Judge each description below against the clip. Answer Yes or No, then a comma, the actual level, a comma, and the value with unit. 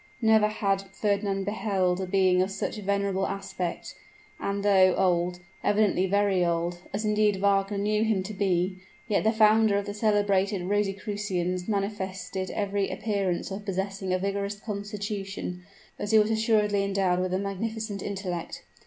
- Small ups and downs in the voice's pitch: Yes, narrow, 1.7 semitones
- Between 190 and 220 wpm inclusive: No, average, 150 wpm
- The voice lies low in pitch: No, high, 200 Hz